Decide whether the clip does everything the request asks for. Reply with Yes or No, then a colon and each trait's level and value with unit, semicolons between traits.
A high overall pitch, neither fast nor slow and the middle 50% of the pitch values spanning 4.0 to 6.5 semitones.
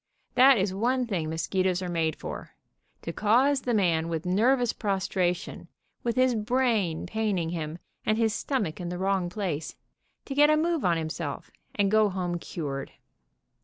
Yes: high, 195 Hz; average, 165 wpm; wide, 5.5 semitones